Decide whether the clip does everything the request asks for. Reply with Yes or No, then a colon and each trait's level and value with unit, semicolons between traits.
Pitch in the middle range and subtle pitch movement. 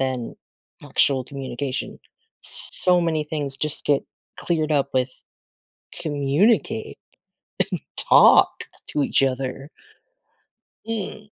No: medium, 145 Hz; average, 3.7 semitones